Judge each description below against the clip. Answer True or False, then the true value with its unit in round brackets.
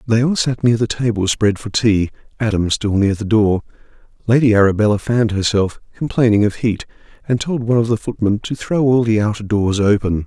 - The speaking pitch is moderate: False (110 Hz)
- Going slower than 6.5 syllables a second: True (5.6 syllables/s)